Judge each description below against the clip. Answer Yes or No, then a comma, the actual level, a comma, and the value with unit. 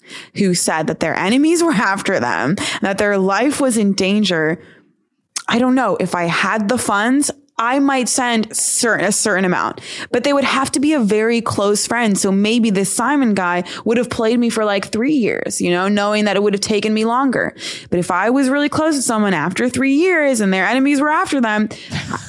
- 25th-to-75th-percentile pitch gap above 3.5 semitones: Yes, average, 5.2 semitones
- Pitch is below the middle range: No, high, 220 Hz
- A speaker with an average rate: No, fast, 215 wpm